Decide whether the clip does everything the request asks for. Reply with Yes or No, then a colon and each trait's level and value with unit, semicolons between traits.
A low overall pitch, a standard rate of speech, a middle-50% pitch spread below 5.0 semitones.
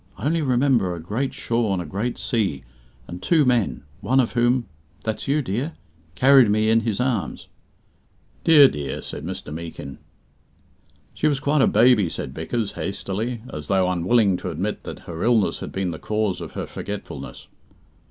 No: low, 110 Hz; average, 170 wpm; average, 5.3 semitones